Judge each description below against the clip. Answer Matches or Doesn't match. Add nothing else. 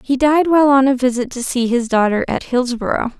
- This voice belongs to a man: Doesn't match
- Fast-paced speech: Matches